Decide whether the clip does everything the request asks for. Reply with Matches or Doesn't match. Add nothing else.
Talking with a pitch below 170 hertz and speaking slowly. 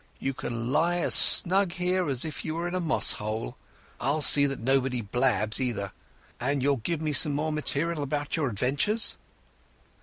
Doesn't match